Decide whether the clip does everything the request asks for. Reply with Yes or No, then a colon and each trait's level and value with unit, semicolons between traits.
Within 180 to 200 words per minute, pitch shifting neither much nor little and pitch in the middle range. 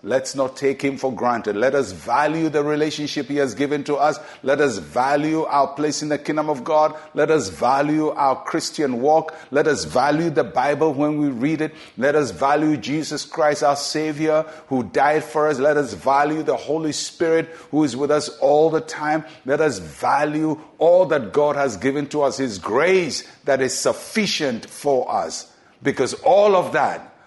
No: average, 190 wpm; narrow, 1.7 semitones; medium, 150 Hz